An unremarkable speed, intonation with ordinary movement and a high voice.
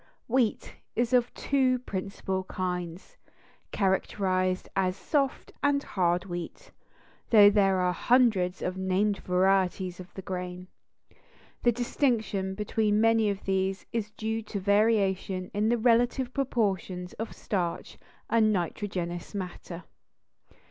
No: slow, 120 wpm; average, 3.5 semitones; high, 195 Hz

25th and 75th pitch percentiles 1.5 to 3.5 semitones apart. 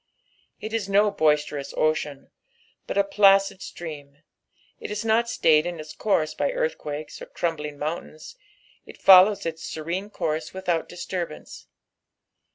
No: average, 4.5 semitones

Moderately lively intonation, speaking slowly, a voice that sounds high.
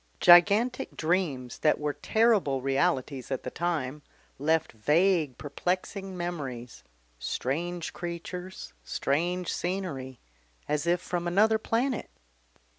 No: average, 4.9 semitones; slow, 105 wpm; medium, 170 Hz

